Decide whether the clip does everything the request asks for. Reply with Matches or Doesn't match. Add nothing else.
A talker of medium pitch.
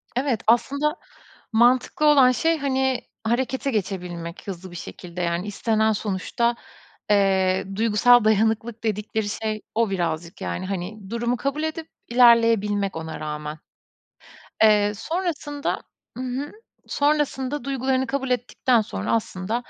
Doesn't match